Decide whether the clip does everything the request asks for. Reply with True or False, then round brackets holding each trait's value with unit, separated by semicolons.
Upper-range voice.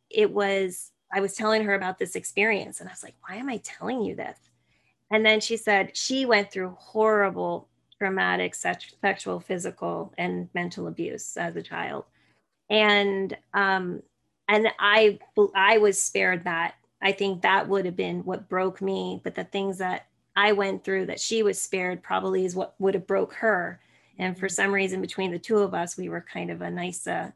True (195 Hz)